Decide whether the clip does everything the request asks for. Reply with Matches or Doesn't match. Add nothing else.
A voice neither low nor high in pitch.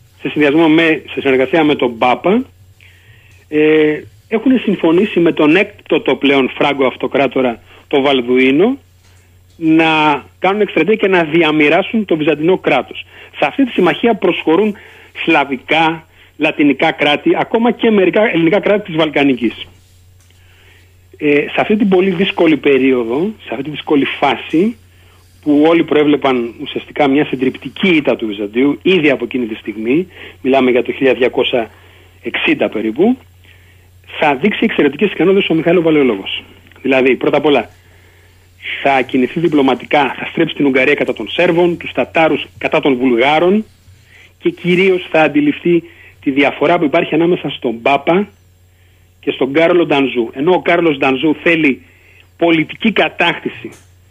Matches